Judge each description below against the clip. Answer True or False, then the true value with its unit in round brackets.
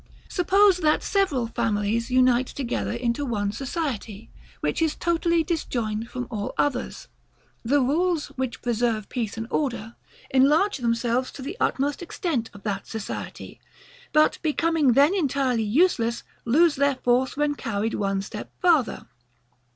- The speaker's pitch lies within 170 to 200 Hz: False (255 Hz)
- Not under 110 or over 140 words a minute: True (135 wpm)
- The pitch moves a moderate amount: True (4.9 semitones)